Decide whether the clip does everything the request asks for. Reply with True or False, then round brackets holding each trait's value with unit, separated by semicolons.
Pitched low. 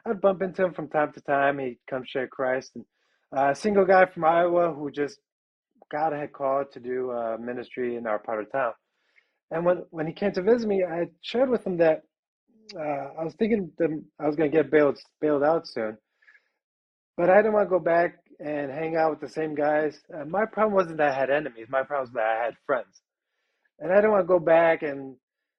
False (155 Hz)